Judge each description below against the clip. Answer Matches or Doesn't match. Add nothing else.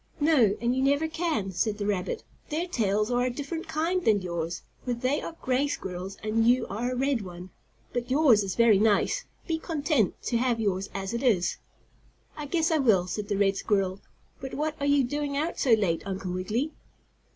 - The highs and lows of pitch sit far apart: Matches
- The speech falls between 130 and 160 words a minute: Doesn't match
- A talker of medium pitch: Doesn't match